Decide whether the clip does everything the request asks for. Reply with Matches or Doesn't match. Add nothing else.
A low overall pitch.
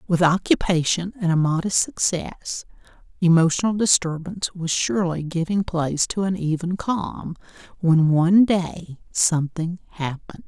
Doesn't match